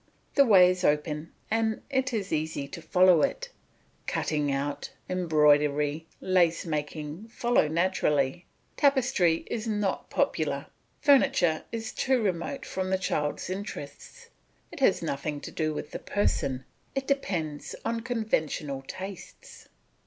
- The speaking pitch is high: No, medium, 175 Hz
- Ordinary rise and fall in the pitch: No, wide, 6.5 semitones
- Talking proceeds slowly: Yes, slow, 130 wpm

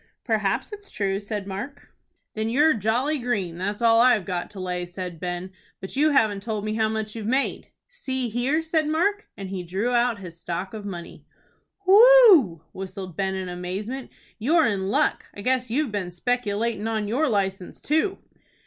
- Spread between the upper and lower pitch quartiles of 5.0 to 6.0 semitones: Yes, wide, 5.4 semitones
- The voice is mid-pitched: No, high, 215 Hz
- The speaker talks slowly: No, average, 175 wpm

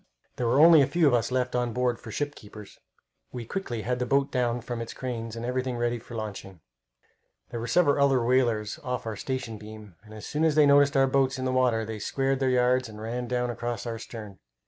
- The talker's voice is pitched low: Yes, low, 125 Hz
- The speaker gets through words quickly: Yes, fast, 235 wpm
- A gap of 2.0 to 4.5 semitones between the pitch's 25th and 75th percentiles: Yes, narrow, 2.5 semitones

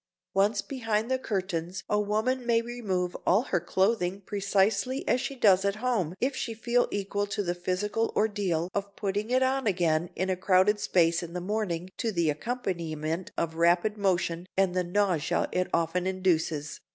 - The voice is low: No, high, 195 Hz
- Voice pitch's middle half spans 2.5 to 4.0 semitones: Yes, average, 3.6 semitones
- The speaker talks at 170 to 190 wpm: Yes, average, 175 wpm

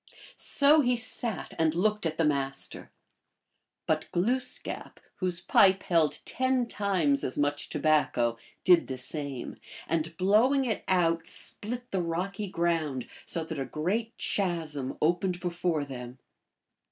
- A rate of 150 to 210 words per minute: No, slow, 135 wpm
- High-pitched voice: No, medium, 170 Hz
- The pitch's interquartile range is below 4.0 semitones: No, average, 5.1 semitones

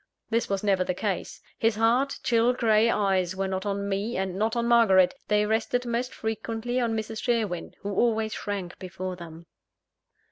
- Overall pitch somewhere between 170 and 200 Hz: No, high, 215 Hz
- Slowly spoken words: No, average, 175 wpm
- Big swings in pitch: No, average, 3.3 semitones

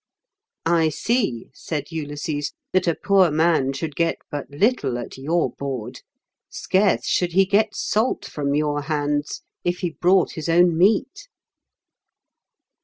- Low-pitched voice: No, medium, 165 Hz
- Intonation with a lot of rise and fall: No, average, 4.2 semitones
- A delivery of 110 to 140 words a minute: Yes, slow, 135 wpm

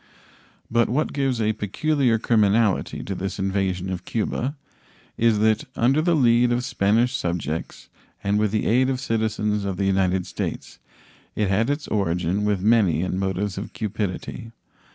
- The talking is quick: No, average, 155 wpm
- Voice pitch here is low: Yes, low, 105 Hz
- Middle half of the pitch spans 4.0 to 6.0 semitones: No, average, 3.4 semitones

